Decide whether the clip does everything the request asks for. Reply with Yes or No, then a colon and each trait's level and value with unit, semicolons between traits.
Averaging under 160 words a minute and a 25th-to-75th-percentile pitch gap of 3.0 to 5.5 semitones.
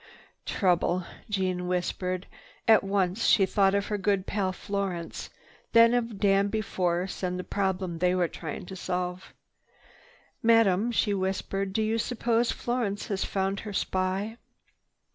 No: average, 140 wpm; narrow, 2.4 semitones